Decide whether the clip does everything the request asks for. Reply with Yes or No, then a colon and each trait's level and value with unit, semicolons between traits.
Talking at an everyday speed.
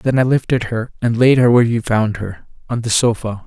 No: fast, 245 wpm